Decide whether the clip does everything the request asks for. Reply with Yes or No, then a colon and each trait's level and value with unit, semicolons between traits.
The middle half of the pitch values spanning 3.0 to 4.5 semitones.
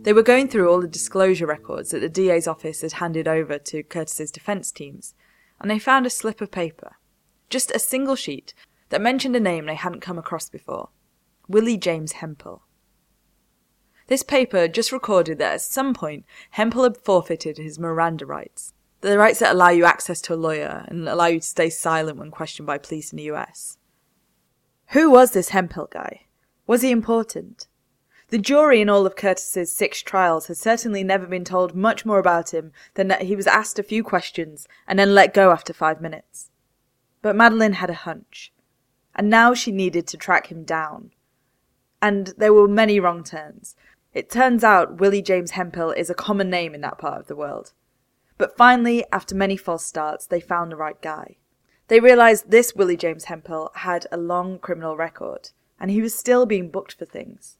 No: average, 4.9 semitones